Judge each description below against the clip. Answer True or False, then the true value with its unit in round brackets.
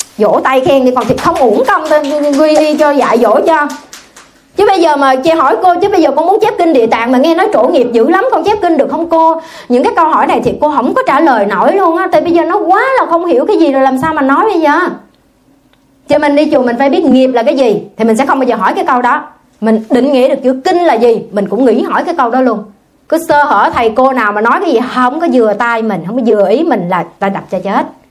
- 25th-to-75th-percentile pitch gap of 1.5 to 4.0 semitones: False (5.1 semitones)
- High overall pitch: True (280 Hz)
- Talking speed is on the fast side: True (295 wpm)